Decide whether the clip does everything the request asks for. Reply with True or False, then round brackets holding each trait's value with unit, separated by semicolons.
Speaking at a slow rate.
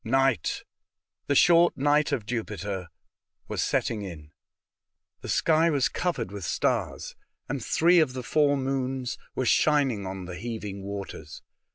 False (150 wpm)